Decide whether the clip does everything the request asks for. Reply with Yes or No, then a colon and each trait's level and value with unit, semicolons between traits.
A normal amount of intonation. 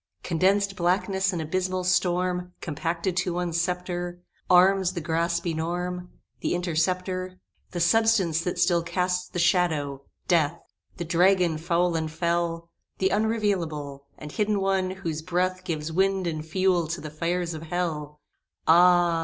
No: narrow, 1.8 semitones